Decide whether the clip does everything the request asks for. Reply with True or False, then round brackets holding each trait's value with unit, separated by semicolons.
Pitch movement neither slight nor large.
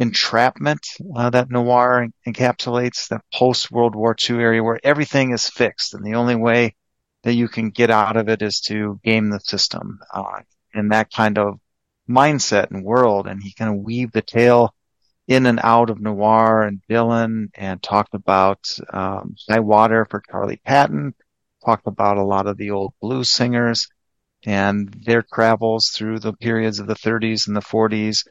False (2.1 semitones)